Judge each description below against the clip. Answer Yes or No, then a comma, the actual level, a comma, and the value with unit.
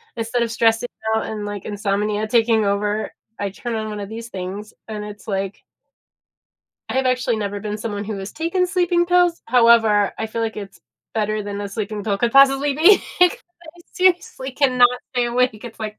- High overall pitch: Yes, high, 220 Hz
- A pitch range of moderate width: Yes, average, 3.4 semitones